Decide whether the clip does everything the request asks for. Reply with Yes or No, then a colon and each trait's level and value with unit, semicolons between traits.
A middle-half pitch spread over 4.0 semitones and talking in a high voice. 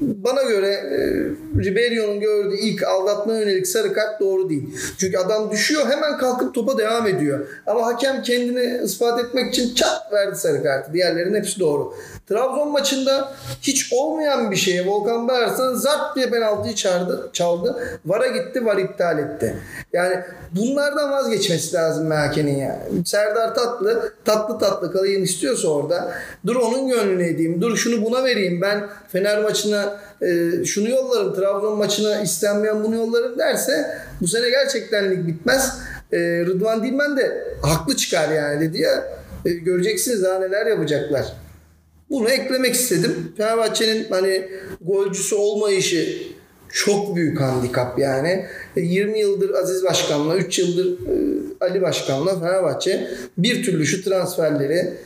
Yes: average, 5.2 semitones; high, 210 Hz